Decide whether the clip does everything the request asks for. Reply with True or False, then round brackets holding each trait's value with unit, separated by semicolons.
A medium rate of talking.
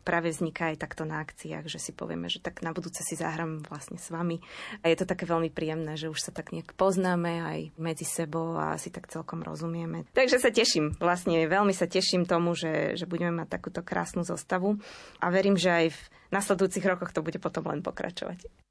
False (210 wpm)